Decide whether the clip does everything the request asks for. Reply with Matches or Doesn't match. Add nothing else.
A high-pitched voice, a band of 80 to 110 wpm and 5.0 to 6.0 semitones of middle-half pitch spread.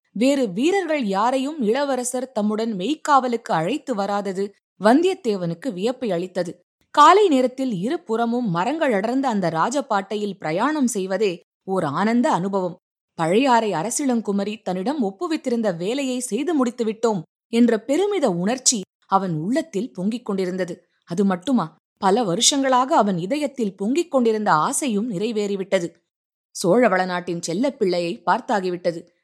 Matches